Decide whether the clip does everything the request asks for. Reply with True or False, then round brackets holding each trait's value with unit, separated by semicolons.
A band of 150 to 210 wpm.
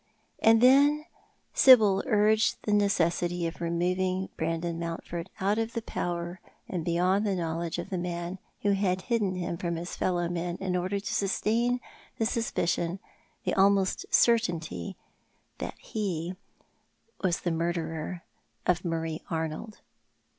False (135 wpm)